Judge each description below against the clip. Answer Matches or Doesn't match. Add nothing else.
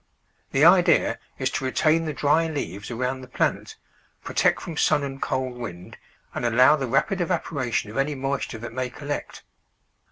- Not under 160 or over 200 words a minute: Matches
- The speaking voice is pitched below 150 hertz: Matches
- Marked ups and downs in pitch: Doesn't match